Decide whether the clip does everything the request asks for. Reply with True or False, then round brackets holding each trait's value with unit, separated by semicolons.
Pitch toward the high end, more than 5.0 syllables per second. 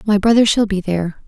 True (205 Hz; 6.2 syllables/s)